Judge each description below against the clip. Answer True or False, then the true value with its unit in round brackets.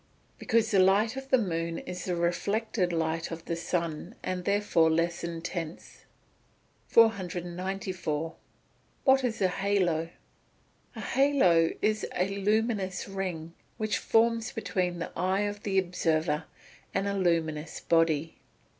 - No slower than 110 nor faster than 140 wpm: True (135 wpm)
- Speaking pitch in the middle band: True (180 Hz)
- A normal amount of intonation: True (3.6 semitones)